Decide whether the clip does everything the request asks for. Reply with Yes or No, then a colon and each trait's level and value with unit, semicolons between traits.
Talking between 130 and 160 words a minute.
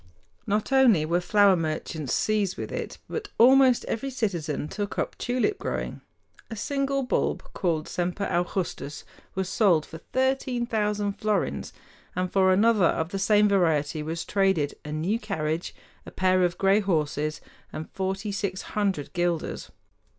Yes: average, 150 wpm